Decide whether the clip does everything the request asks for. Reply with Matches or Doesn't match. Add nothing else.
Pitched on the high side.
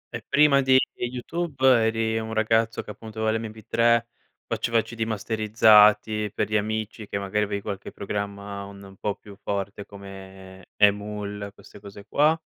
Doesn't match